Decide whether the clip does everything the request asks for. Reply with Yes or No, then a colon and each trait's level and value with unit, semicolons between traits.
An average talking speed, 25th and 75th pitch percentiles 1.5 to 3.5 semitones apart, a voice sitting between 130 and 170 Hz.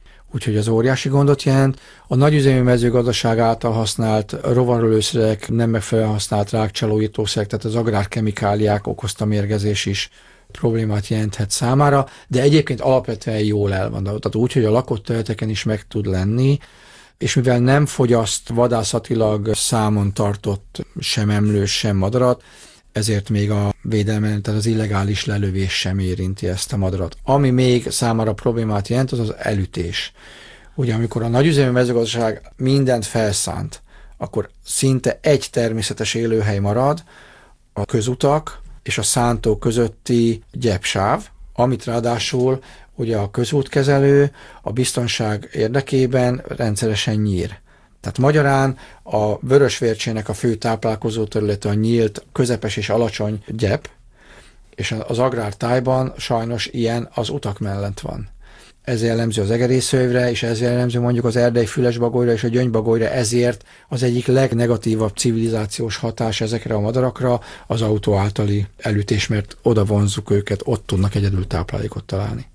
No: average, 130 wpm; average, 2.8 semitones; low, 115 Hz